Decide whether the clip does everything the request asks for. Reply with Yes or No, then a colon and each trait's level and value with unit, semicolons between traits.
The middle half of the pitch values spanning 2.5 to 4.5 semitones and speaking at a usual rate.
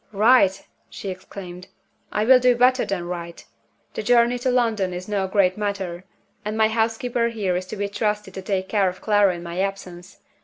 Yes: average, 3.3 semitones; average, 190 wpm